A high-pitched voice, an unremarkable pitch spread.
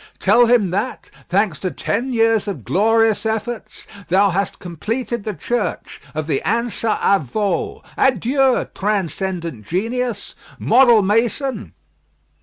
Yes: high, 215 Hz; average, 4.0 semitones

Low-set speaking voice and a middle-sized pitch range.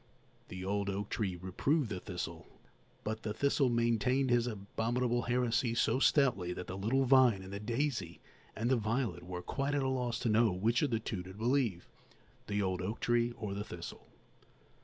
Yes: low, 115 Hz; average, 4.3 semitones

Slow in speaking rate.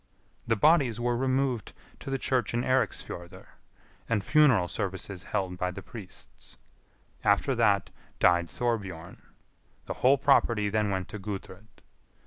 Yes: slow, 130 wpm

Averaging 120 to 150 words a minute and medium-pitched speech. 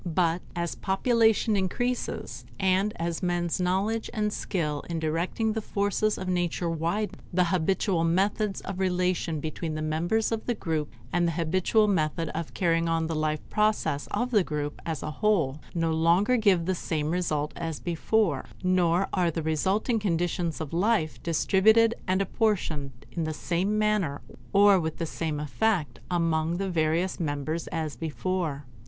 No: average, 160 wpm; medium, 175 Hz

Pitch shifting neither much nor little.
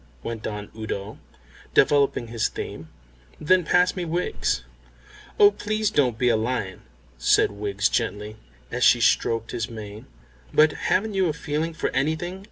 No: wide, 8.2 semitones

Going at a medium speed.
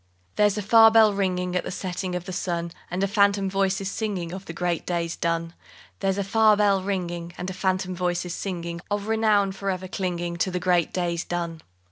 No: fast, 220 wpm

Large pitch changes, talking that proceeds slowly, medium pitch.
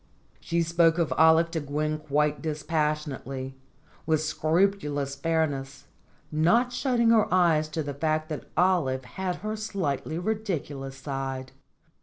No: average, 3.5 semitones; slow, 125 wpm; medium, 155 Hz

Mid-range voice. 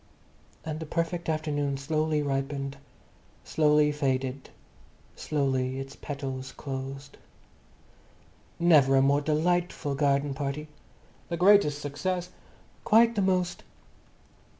Yes: medium, 145 Hz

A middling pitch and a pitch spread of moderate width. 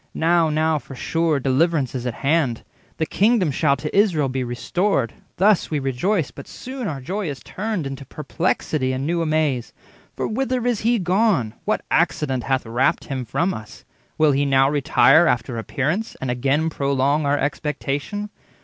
Yes: medium, 150 Hz; average, 4.7 semitones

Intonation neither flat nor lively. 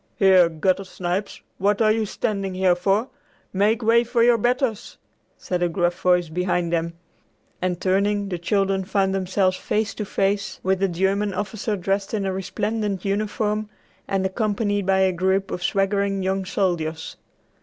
No: narrow, 2.0 semitones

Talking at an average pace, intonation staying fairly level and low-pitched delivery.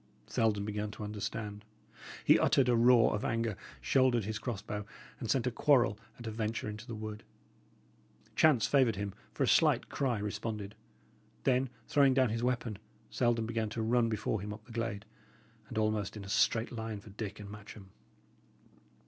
Yes: average, 175 wpm; narrow, 2.2 semitones; low, 110 Hz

